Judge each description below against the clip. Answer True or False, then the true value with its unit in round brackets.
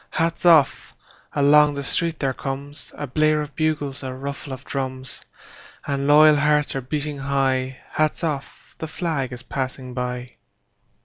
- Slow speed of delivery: True (125 wpm)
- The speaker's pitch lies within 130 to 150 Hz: True (140 Hz)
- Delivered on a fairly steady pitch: True (2.3 semitones)